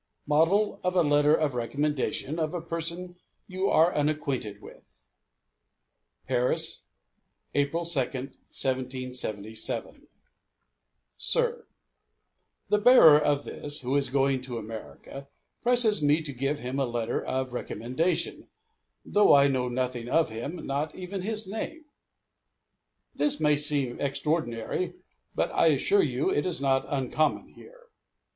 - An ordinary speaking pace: No, slow, 125 wpm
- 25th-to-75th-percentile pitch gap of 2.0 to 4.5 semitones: No, wide, 5.4 semitones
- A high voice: No, medium, 145 Hz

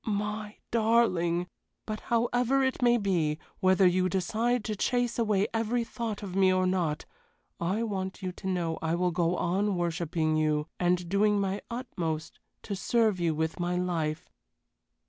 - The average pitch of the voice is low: No, high, 190 Hz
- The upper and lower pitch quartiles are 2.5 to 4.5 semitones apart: Yes, average, 4.0 semitones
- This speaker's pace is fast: No, average, 160 wpm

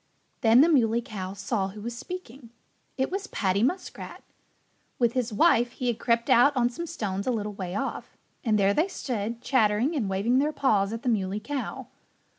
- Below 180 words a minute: No, average, 190 wpm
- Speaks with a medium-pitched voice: No, high, 235 Hz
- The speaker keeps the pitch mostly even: No, average, 4.1 semitones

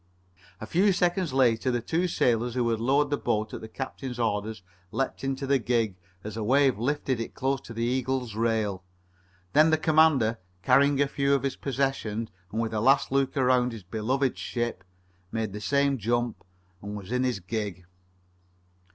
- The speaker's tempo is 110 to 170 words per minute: No, average, 180 wpm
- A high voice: No, low, 125 Hz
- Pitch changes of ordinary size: Yes, average, 3.7 semitones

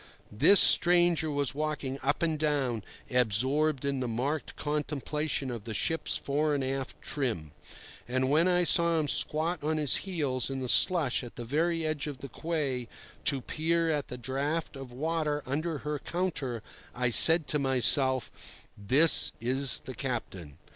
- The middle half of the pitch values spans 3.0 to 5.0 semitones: Yes, average, 3.4 semitones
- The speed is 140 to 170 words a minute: Yes, average, 160 wpm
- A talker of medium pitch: Yes, medium, 145 Hz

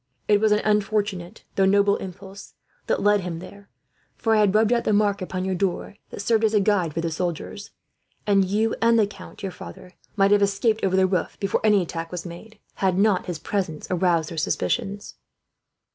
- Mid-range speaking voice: No, high, 200 Hz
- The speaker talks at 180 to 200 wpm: Yes, average, 195 wpm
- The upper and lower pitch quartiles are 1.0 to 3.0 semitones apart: Yes, narrow, 2.5 semitones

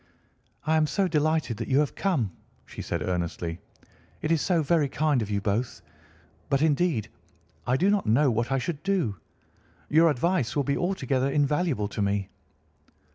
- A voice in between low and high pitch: Yes, medium, 145 Hz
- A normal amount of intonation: No, wide, 5.7 semitones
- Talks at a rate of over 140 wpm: Yes, average, 170 wpm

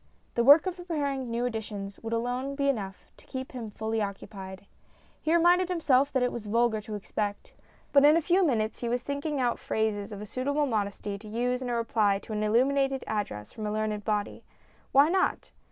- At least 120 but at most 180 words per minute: No, average, 200 wpm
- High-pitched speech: Yes, high, 235 Hz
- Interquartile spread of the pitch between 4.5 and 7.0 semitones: Yes, average, 4.8 semitones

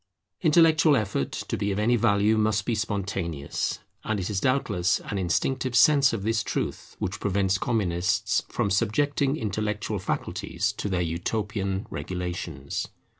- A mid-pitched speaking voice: No, low, 105 Hz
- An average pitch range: Yes, average, 3.4 semitones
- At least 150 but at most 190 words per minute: No, average, 140 wpm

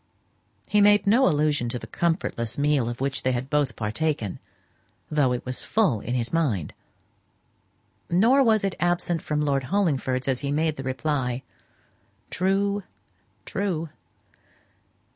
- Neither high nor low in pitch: Yes, medium, 150 Hz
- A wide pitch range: Yes, wide, 5.7 semitones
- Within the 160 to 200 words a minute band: No, slow, 135 wpm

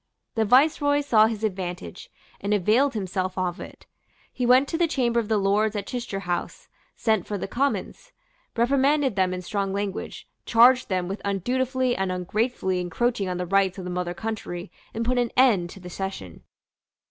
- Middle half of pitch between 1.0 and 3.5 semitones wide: No, average, 4.9 semitones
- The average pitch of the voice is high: Yes, high, 210 Hz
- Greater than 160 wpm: Yes, average, 180 wpm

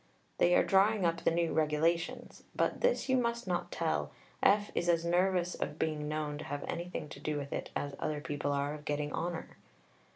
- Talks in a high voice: No, medium, 165 Hz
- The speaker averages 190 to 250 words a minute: Yes, average, 200 wpm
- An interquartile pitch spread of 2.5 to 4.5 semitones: Yes, average, 3.1 semitones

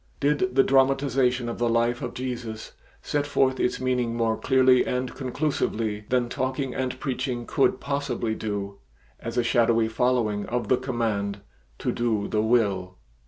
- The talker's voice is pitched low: Yes, low, 120 Hz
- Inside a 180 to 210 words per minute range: No, average, 155 wpm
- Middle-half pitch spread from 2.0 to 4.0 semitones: Yes, narrow, 2.6 semitones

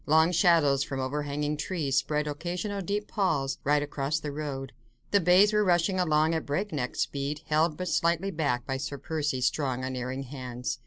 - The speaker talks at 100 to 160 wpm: No, average, 170 wpm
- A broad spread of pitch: No, average, 3.8 semitones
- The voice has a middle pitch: Yes, medium, 150 Hz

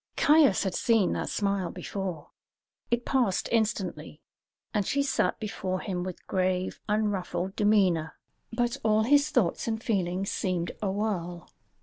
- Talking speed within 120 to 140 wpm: Yes, slow, 135 wpm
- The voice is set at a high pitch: Yes, high, 200 Hz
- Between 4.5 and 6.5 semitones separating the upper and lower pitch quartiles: No, average, 3.5 semitones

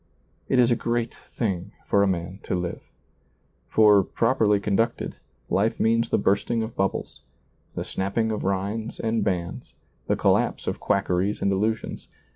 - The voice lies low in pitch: Yes, low, 105 Hz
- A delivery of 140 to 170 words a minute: Yes, average, 150 wpm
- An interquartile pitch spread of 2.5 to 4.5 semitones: Yes, average, 2.8 semitones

